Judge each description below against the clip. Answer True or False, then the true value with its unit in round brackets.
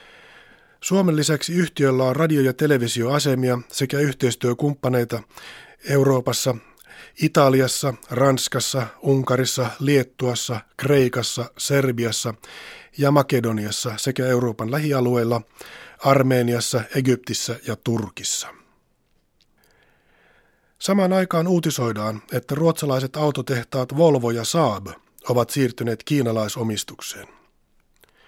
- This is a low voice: True (130 Hz)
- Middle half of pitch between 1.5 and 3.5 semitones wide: True (3.1 semitones)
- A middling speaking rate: False (80 wpm)